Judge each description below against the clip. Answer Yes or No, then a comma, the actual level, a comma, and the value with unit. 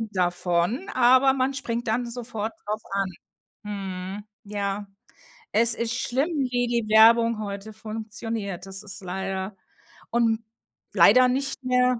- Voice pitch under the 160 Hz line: No, high, 220 Hz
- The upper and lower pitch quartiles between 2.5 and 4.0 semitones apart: Yes, average, 3.5 semitones